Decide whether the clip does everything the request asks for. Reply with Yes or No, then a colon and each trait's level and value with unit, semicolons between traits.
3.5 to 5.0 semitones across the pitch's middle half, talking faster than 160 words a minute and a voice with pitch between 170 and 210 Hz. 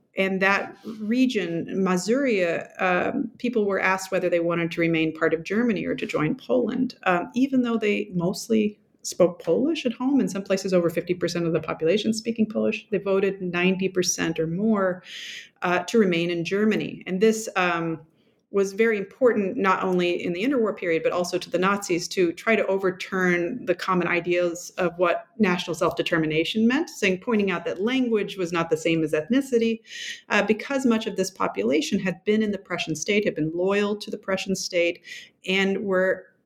Yes: average, 3.9 semitones; average, 185 wpm; high, 190 Hz